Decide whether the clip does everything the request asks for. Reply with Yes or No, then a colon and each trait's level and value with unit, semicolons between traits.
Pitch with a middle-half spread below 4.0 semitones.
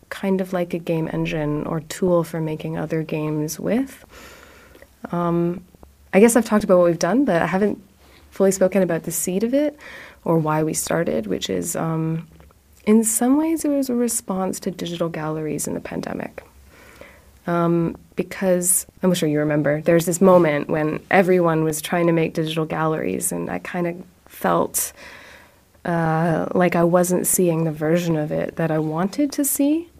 Yes: average, 3.3 semitones